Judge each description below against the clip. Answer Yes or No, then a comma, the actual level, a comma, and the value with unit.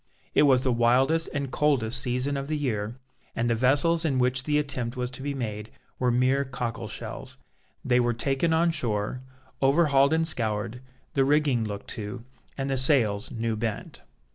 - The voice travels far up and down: No, average, 3.3 semitones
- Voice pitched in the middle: No, low, 130 Hz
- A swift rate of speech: No, average, 175 wpm